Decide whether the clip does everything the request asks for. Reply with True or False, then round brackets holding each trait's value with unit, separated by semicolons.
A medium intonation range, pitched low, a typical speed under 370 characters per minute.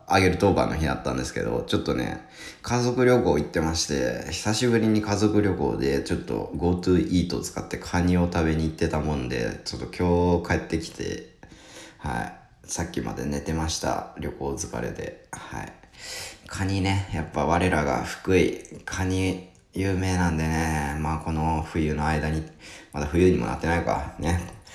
True (3.1 semitones; 85 Hz; 330 characters per minute)